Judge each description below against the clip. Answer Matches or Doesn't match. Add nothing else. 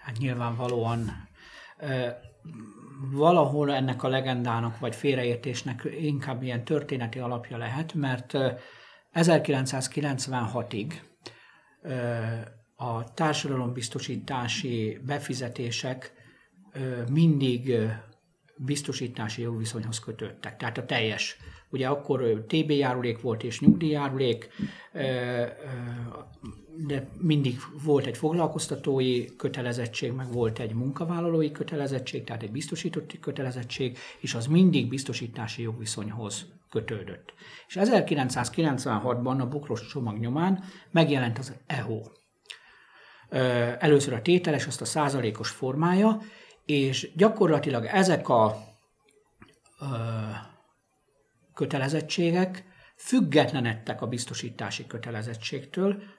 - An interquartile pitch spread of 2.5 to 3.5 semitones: Doesn't match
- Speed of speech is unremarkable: Doesn't match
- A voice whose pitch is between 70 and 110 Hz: Doesn't match